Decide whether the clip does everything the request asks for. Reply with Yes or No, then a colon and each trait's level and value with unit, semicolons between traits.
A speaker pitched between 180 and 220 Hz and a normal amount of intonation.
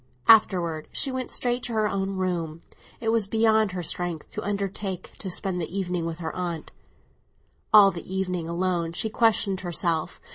Yes: medium, 185 Hz; average, 3.7 semitones